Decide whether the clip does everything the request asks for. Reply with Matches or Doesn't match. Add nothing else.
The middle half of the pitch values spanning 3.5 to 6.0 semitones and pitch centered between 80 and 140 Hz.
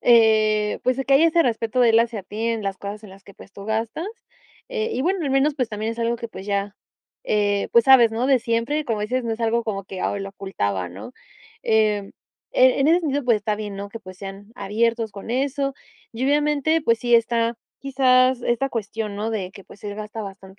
Doesn't match